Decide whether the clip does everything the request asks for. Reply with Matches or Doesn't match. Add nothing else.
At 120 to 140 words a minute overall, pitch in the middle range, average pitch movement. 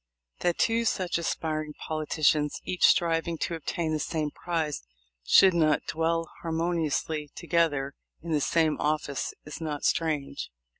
Doesn't match